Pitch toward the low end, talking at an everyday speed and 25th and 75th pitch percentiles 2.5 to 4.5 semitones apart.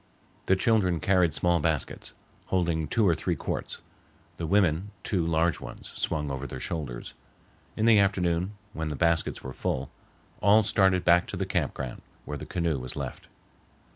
Yes: very low, 85 Hz; average, 170 wpm; average, 3.6 semitones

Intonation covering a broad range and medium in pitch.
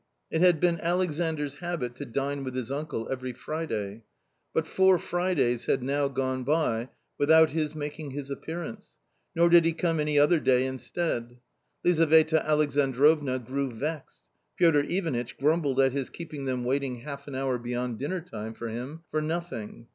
No: average, 3.9 semitones; medium, 145 Hz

